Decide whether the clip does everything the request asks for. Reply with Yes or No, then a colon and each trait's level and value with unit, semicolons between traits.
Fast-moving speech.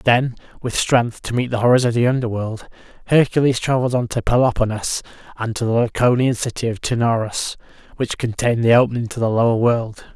No: average, 175 wpm